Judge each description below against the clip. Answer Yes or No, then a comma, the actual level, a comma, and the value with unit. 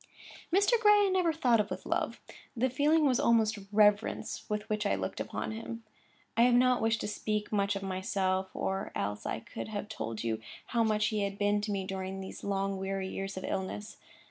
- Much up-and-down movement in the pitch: No, average, 3.1 semitones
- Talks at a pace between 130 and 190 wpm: No, fast, 205 wpm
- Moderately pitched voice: No, high, 210 Hz